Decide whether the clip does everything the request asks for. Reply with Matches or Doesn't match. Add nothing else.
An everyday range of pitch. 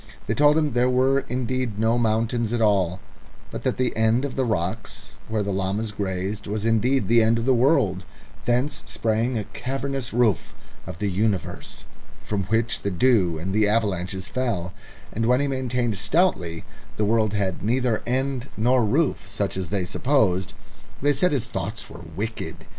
Matches